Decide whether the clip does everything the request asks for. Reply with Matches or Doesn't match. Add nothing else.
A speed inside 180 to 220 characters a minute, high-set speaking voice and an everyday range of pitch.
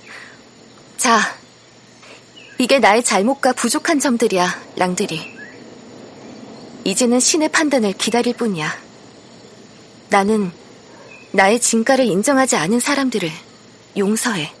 Matches